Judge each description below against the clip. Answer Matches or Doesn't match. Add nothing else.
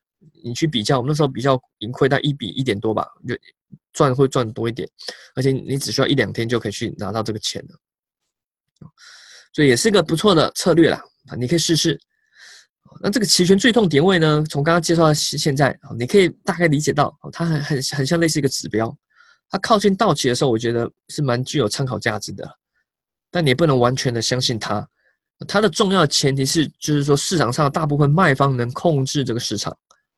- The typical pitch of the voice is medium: Matches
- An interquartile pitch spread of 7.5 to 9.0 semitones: Doesn't match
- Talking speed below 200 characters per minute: Doesn't match